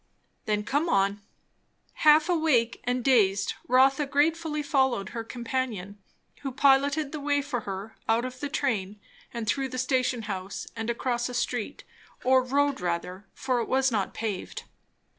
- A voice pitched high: Yes, very high, 255 Hz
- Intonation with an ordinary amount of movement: Yes, average, 4.4 semitones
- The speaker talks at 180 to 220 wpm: No, average, 155 wpm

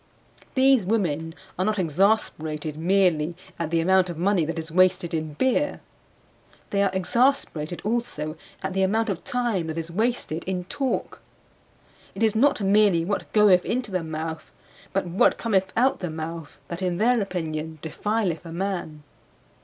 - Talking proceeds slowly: No, average, 160 wpm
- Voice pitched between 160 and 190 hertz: Yes, medium, 185 Hz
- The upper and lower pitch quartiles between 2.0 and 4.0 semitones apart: No, average, 4.5 semitones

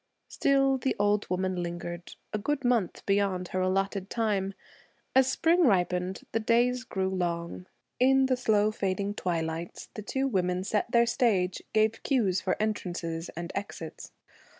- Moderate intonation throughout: Yes, average, 4.5 semitones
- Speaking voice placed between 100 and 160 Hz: No, high, 200 Hz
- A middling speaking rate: Yes, average, 150 wpm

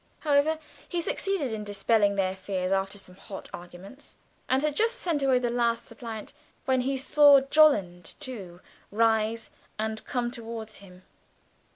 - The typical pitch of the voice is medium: No, high, 230 Hz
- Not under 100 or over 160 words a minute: Yes, average, 150 wpm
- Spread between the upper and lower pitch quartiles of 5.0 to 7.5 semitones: Yes, wide, 5.4 semitones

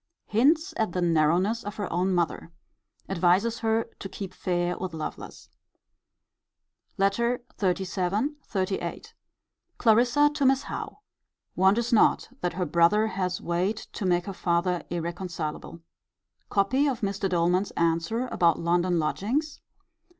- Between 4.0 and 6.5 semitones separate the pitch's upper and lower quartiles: Yes, average, 4.3 semitones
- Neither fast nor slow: No, slow, 125 wpm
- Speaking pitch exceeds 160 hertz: Yes, high, 190 Hz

